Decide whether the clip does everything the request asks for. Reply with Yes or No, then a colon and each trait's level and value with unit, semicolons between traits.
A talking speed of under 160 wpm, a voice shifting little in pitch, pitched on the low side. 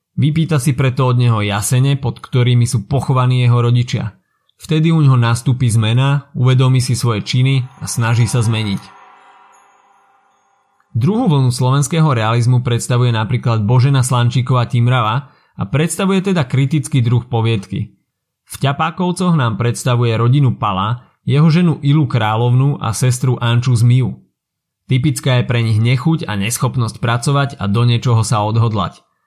No: average, 135 wpm; average, 3.1 semitones; low, 125 Hz